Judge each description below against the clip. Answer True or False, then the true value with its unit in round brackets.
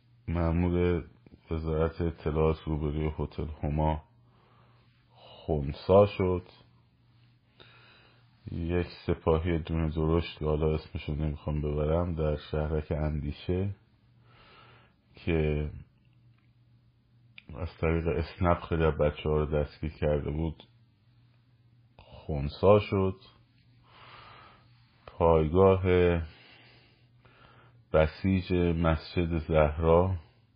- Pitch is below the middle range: True (90 Hz)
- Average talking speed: False (75 wpm)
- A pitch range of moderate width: False (7.0 semitones)